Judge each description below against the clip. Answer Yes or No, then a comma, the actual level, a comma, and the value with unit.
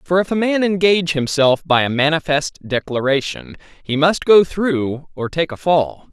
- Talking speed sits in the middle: Yes, average, 175 wpm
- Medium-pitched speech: Yes, medium, 155 Hz